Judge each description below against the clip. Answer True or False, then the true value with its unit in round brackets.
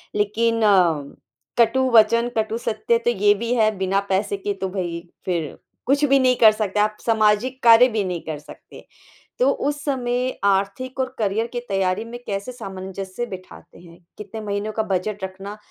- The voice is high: True (215 Hz)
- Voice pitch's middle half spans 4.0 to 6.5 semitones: False (3.5 semitones)